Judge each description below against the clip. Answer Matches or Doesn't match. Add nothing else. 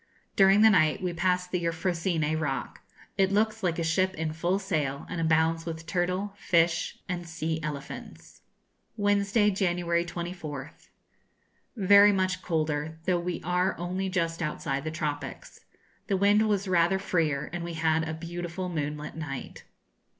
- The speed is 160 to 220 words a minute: Doesn't match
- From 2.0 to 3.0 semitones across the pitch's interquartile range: Matches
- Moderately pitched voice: Matches